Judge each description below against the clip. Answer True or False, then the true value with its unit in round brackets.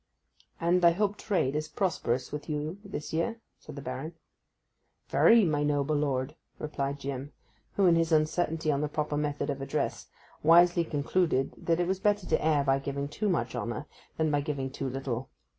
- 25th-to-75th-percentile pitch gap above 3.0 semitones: True (3.5 semitones)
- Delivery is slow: False (180 wpm)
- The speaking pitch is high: False (150 Hz)